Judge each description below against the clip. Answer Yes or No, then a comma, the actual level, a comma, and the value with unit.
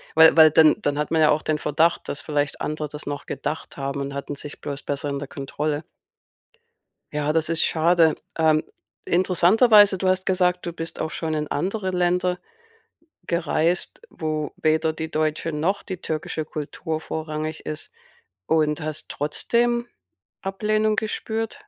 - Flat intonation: No, average, 3.1 semitones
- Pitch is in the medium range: Yes, medium, 160 Hz